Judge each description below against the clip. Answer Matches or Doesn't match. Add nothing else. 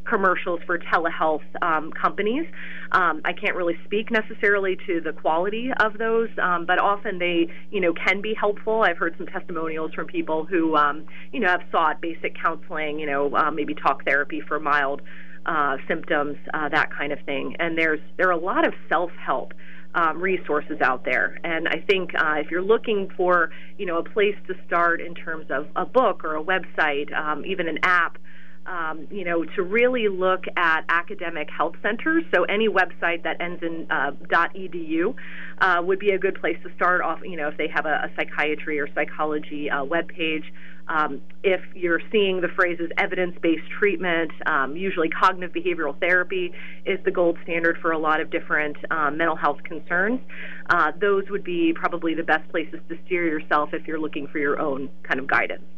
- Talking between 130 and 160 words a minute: Doesn't match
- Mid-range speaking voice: Matches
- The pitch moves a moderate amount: Matches